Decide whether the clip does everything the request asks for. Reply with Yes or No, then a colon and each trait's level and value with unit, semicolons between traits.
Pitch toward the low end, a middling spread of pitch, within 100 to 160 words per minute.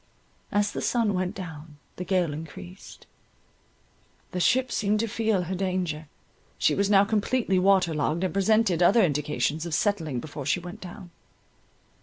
No: medium, 180 Hz; average, 4.3 semitones; average, 155 wpm